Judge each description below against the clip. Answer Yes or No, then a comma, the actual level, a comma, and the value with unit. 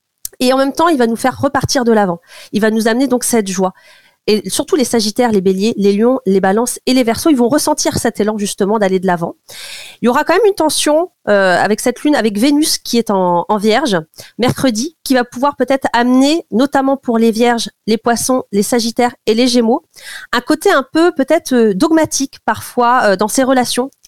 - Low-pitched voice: No, high, 245 Hz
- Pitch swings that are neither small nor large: Yes, average, 4.1 semitones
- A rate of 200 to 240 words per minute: Yes, average, 215 wpm